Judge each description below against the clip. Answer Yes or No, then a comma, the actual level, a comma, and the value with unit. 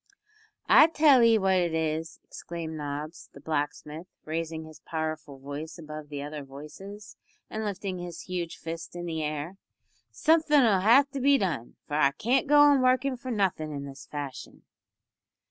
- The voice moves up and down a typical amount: No, wide, 6.4 semitones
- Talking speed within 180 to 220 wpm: No, average, 165 wpm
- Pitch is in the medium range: Yes, medium, 165 Hz